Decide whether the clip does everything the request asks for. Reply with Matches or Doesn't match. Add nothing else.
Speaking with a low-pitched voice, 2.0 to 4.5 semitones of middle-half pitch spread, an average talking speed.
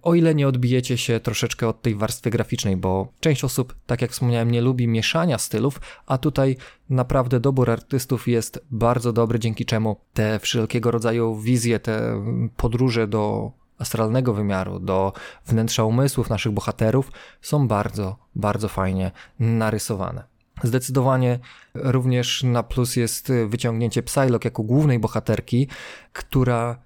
Matches